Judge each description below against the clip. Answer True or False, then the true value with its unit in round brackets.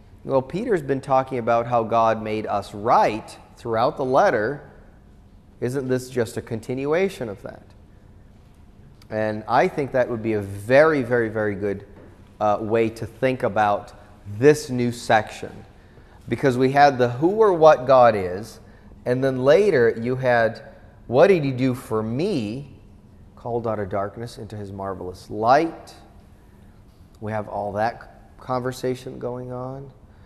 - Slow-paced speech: False (145 wpm)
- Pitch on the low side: True (110 Hz)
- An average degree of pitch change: True (4.0 semitones)